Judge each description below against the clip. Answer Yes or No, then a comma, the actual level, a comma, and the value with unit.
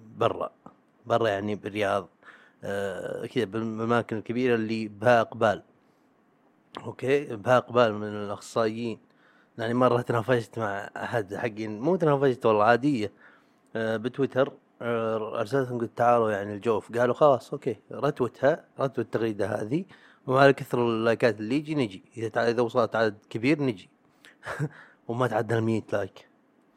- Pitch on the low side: Yes, low, 115 Hz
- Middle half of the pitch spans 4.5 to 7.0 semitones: No, narrow, 2.4 semitones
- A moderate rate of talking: Yes, average, 125 wpm